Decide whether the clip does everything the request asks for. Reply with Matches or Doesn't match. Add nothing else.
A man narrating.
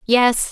Doesn't match